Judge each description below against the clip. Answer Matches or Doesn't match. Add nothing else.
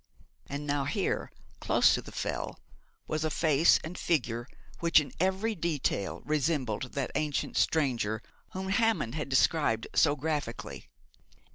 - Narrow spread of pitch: Doesn't match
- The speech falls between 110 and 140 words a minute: Matches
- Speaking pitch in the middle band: Matches